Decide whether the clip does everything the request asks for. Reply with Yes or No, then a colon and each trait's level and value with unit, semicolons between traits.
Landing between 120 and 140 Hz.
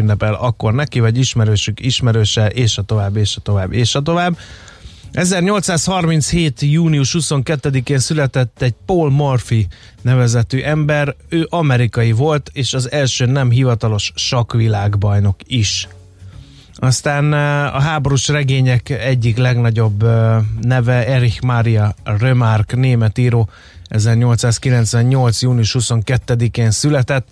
Yes: low, 125 Hz